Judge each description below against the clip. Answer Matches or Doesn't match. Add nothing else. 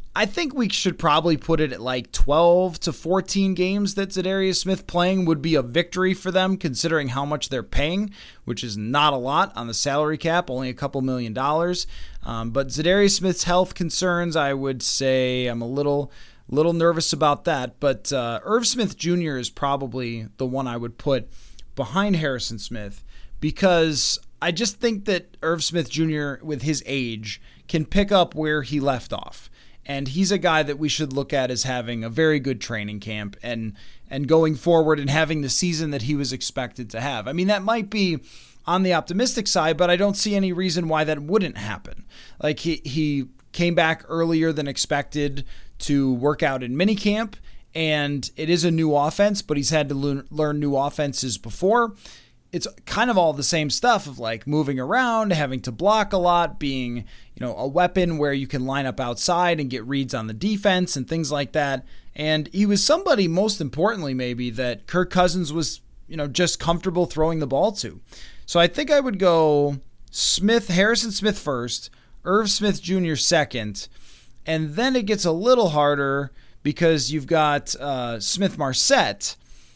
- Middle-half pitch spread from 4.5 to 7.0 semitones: Matches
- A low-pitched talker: Doesn't match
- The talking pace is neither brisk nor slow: Matches